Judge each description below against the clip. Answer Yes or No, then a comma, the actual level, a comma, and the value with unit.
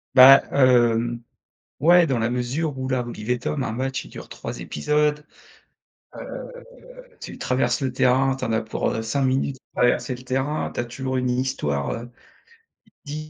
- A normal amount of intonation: No, narrow, 2.3 semitones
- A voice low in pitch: Yes, low, 130 Hz